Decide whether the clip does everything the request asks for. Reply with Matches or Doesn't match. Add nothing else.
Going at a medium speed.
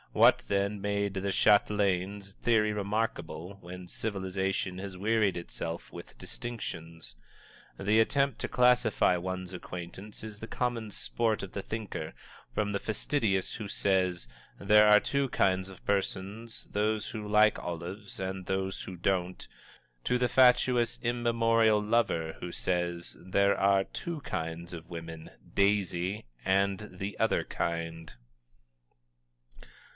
Doesn't match